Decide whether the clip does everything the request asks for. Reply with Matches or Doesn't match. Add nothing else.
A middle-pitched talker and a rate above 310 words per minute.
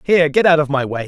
Matches